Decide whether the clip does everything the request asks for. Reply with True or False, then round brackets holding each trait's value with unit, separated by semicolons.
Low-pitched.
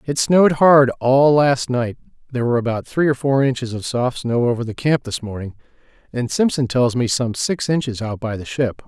True (130 Hz)